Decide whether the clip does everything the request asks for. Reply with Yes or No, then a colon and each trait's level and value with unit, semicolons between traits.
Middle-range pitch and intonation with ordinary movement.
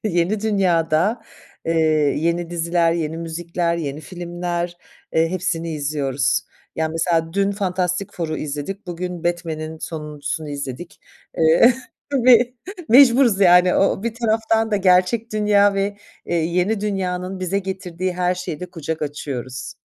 Yes: medium, 175 Hz; average, 3.4 semitones